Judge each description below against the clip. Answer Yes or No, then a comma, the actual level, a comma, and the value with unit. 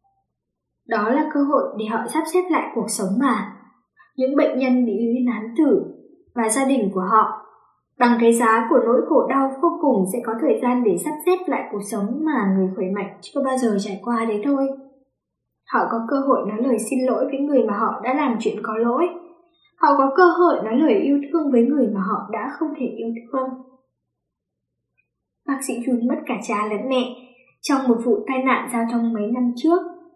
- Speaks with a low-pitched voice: No, very high, 250 Hz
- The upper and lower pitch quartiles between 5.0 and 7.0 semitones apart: No, average, 4.1 semitones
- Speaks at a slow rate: No, average, 210 wpm